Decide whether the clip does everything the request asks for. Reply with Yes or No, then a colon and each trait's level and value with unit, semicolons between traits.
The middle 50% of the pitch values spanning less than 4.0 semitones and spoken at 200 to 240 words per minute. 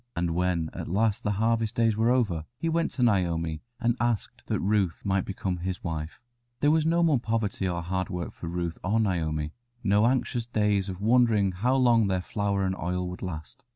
No: average, 4.3 semitones; fast, 205 wpm